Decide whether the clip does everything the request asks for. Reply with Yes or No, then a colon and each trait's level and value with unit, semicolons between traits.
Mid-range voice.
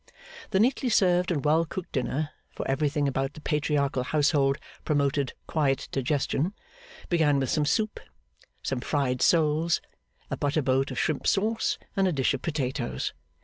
Yes: medium, 150 Hz